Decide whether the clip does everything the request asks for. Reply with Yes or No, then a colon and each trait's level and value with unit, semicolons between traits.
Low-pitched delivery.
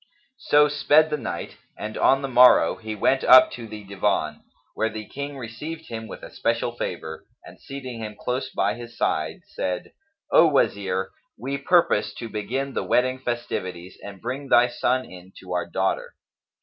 Yes: low, 120 Hz